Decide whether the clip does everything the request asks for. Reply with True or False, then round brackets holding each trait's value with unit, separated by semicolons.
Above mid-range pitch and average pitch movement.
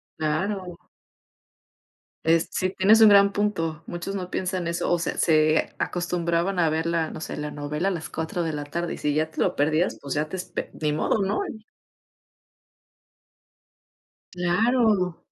False (170 Hz; 3.1 semitones)